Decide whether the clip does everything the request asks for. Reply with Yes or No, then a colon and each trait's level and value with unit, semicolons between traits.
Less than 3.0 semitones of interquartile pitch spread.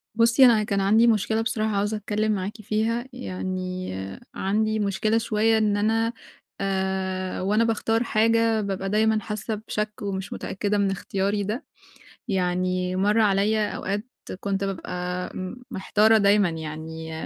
Yes: narrow, 2.4 semitones